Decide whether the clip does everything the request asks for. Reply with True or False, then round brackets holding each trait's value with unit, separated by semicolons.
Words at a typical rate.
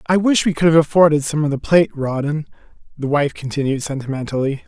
True (195 wpm)